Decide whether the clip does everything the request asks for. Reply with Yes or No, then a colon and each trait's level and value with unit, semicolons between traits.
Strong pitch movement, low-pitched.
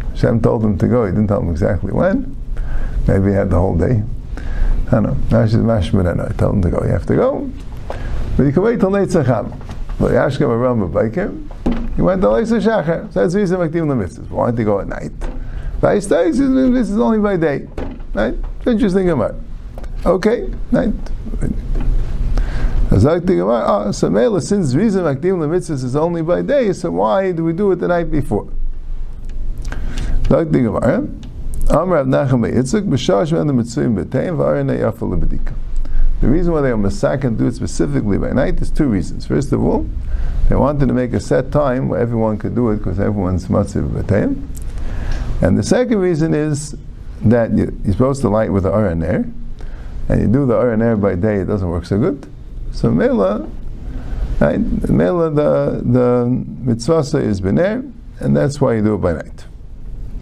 Yes: wide, 8.5 semitones; low, 120 Hz